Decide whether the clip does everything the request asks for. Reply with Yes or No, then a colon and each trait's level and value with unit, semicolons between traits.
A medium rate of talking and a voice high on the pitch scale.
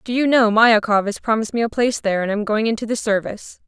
No: fast, 260 wpm; high, 220 Hz